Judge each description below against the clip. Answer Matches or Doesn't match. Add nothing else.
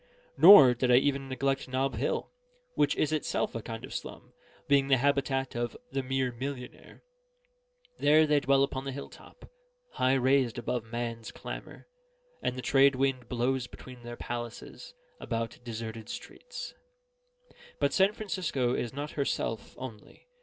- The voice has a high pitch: Doesn't match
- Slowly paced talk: Doesn't match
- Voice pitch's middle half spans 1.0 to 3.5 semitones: Matches